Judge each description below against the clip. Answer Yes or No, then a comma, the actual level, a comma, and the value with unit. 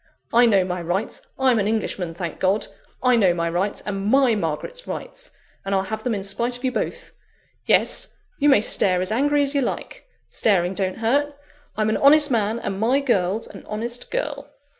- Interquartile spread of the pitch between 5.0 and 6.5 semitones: Yes, wide, 5.5 semitones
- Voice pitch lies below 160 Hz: No, high, 220 Hz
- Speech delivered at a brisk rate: No, average, 195 wpm